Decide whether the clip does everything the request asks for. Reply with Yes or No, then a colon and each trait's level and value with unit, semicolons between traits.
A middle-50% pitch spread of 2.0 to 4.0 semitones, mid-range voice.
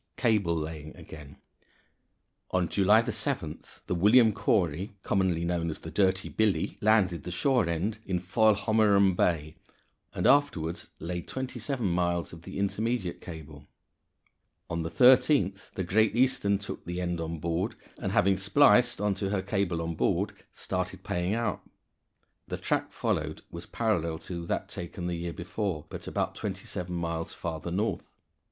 No: average, 3.6 semitones; very low, 90 Hz